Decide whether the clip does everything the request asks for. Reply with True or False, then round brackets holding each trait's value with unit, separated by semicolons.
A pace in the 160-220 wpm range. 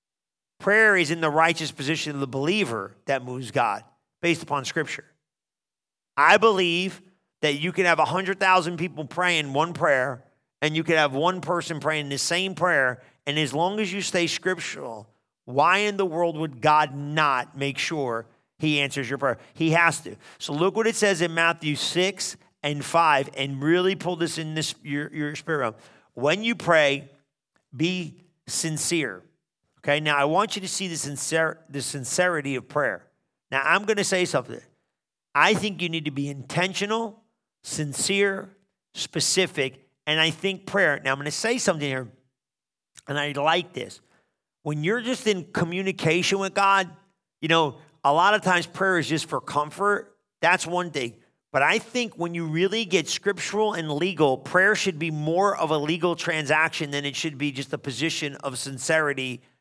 True (175 wpm)